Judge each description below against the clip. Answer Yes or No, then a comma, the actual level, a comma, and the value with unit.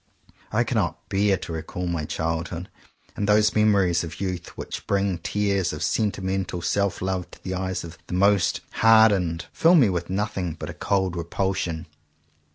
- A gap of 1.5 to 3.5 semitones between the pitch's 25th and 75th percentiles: Yes, average, 2.8 semitones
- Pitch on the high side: No, very low, 95 Hz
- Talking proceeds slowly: No, average, 165 wpm